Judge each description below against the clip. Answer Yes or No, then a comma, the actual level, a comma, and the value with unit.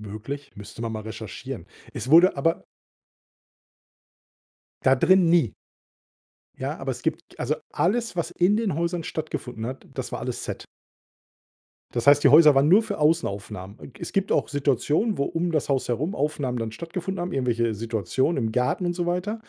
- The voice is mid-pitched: Yes, medium, 145 Hz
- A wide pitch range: Yes, wide, 6.7 semitones